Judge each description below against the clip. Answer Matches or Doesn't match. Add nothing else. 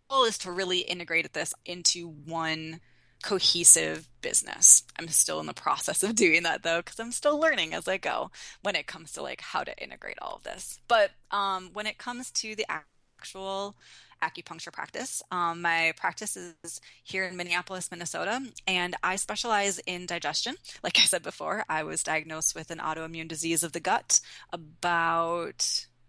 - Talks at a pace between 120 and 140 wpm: Doesn't match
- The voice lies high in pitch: Doesn't match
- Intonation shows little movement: Doesn't match